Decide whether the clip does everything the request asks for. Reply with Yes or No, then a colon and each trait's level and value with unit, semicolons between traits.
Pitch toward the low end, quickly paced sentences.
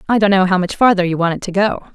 No: high, 190 Hz; fast, 340 wpm